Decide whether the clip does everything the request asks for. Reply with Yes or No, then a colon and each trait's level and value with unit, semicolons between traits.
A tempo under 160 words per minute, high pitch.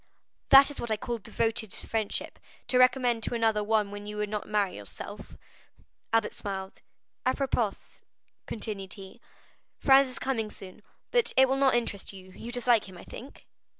No: average, 170 wpm; high, 225 Hz